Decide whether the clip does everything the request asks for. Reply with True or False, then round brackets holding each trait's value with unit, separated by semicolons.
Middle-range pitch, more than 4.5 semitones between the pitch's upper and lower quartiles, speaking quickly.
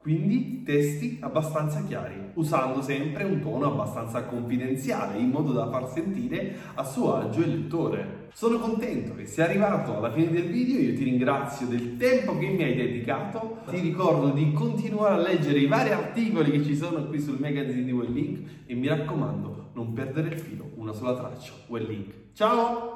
True (150 Hz; 5.3 semitones; 180 wpm)